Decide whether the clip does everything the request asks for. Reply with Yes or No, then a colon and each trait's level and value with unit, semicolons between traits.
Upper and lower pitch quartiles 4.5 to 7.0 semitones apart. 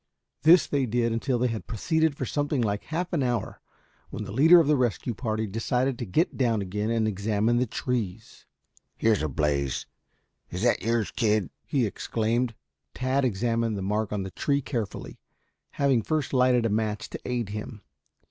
No: average, 3.6 semitones